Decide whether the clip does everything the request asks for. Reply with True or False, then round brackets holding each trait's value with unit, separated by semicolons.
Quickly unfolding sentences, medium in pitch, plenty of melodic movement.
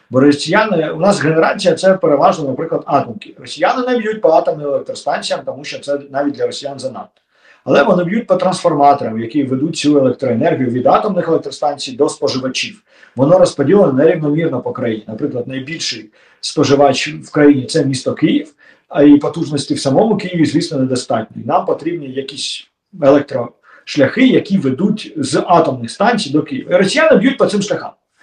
True (160 wpm; 155 Hz; 6.0 semitones)